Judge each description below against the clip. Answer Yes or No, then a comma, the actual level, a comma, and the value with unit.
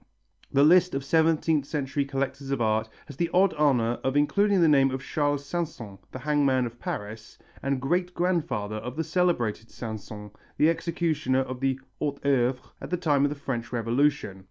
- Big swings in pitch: No, average, 4.3 semitones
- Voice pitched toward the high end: No, medium, 140 Hz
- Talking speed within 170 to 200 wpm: Yes, average, 180 wpm